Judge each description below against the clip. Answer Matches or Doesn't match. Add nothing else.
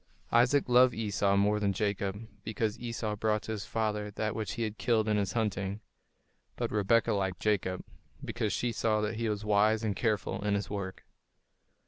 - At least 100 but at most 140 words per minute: Doesn't match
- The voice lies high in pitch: Doesn't match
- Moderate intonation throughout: Doesn't match